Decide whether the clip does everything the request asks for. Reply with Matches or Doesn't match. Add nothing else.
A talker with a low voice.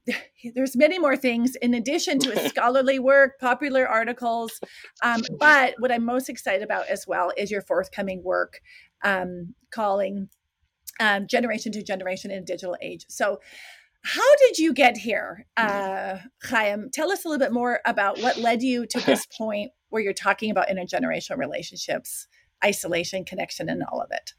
Doesn't match